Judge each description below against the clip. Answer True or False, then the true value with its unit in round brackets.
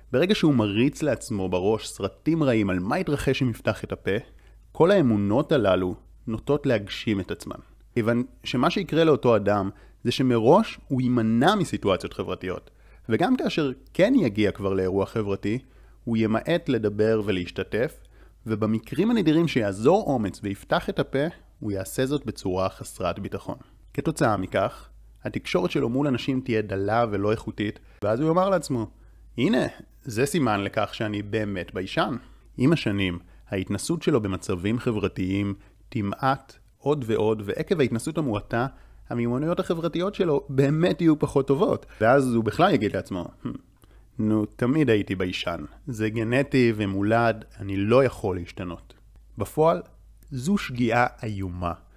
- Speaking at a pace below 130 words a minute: False (135 wpm)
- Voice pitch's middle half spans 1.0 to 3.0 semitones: False (5.4 semitones)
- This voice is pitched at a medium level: False (110 Hz)